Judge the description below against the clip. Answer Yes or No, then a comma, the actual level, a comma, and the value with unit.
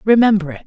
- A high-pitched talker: Yes, high, 205 Hz